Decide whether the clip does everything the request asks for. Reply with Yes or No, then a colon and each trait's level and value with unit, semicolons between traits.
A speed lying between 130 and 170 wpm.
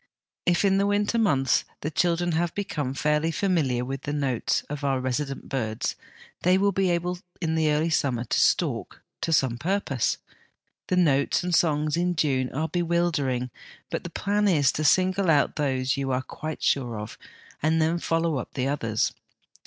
No: average, 185 wpm